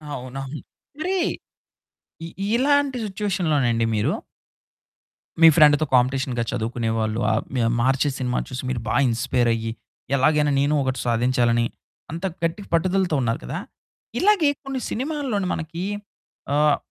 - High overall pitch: No, medium, 140 Hz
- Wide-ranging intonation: Yes, wide, 7.5 semitones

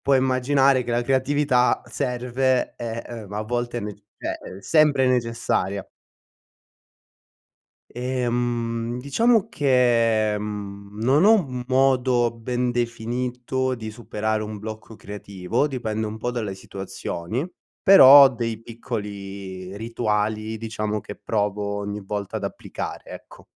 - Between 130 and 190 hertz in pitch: No, low, 115 Hz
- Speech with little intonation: No, average, 3.2 semitones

